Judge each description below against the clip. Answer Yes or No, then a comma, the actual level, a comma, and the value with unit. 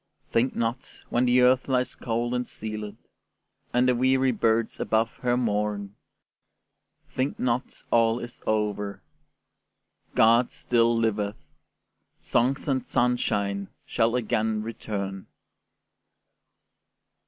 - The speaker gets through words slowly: Yes, slow, 105 wpm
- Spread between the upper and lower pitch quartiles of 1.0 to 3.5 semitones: Yes, narrow, 2.6 semitones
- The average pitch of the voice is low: Yes, low, 115 Hz